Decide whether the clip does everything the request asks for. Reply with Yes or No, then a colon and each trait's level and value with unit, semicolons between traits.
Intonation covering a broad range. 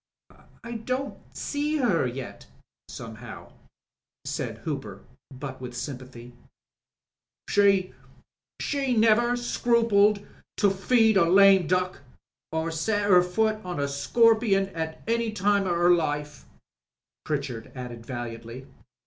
Yes: wide, 7.8 semitones